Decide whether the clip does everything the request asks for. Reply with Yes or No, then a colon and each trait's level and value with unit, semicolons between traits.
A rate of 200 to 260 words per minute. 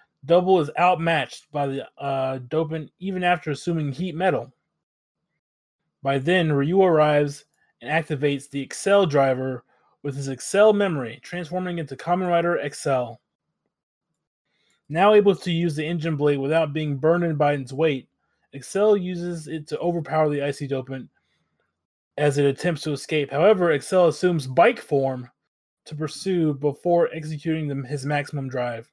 No: average, 145 wpm